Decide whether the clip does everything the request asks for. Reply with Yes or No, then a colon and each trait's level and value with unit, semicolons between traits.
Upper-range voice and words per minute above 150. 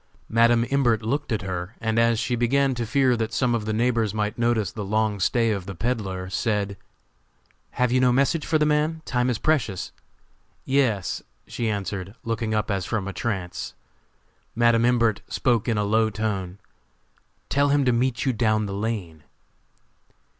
No: low, 115 Hz; average, 175 wpm